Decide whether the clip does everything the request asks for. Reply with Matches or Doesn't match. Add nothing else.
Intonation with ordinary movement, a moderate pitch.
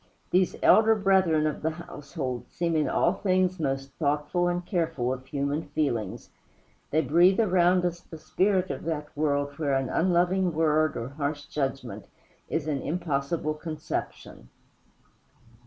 Matches